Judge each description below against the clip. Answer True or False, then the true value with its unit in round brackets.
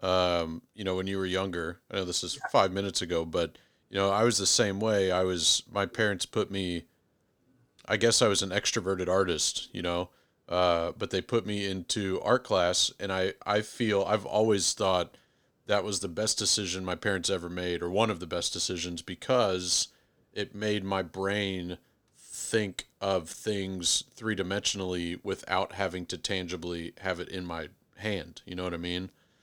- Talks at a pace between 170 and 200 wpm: True (185 wpm)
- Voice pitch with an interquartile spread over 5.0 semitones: False (2.4 semitones)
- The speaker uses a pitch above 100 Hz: False (95 Hz)